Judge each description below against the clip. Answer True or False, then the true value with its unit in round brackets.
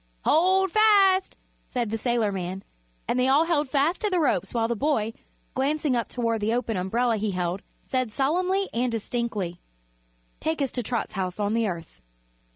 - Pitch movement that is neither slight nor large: False (6.2 semitones)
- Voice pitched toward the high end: True (240 Hz)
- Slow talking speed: False (170 wpm)